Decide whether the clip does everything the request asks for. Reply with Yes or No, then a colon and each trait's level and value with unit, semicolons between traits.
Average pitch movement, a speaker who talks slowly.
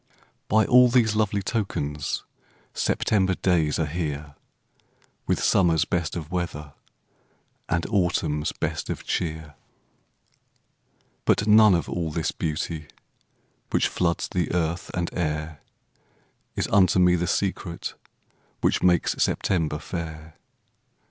Yes: average, 3.2 semitones; slow, 115 wpm